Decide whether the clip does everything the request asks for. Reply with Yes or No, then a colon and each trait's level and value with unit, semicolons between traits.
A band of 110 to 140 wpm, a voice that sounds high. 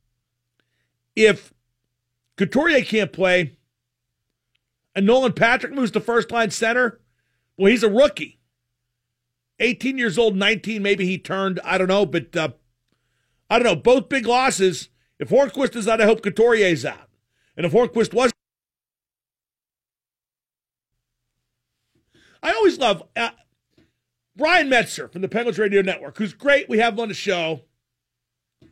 Yes: slow, 135 wpm; high, 195 Hz